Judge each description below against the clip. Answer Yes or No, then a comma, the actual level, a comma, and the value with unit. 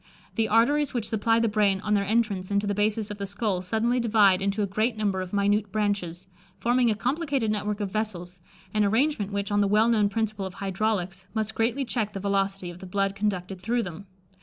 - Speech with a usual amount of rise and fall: No, narrow, 2.1 semitones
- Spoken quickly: Yes, fast, 210 wpm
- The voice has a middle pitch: No, high, 205 Hz